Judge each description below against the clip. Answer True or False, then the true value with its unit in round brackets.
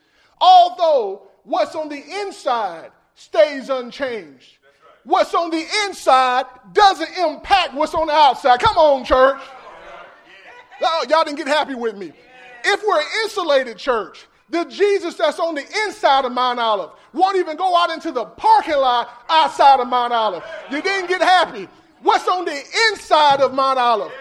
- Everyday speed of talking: True (160 wpm)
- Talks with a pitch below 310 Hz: False (320 Hz)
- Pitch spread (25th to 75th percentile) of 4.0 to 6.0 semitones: True (5.5 semitones)